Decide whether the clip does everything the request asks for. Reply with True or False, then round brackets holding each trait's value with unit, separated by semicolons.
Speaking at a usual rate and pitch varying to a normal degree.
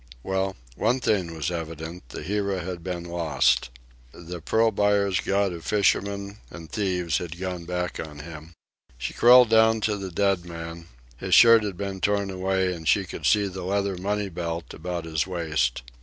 True (175 wpm; 3.2 semitones)